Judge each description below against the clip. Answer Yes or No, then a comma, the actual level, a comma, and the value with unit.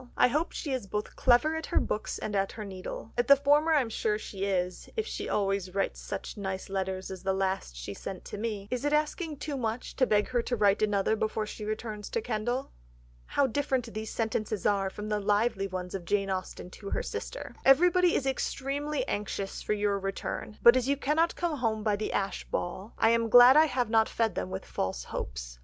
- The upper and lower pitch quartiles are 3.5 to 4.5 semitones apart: No, average, 4.9 semitones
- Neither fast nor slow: No, fast, 220 wpm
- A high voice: Yes, high, 215 Hz